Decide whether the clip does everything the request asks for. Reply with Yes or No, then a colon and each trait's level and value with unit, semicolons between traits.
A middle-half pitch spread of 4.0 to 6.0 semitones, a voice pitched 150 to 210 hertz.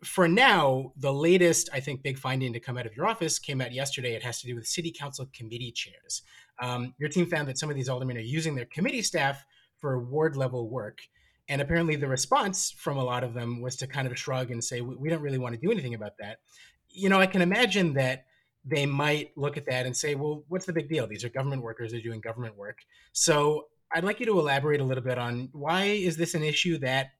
No: average, 4.5 semitones; low, 135 Hz